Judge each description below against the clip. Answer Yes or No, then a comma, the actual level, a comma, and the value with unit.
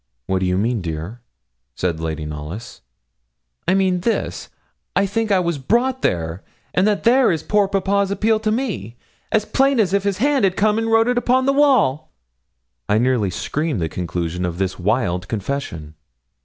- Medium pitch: Yes, medium, 170 Hz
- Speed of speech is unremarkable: Yes, average, 175 wpm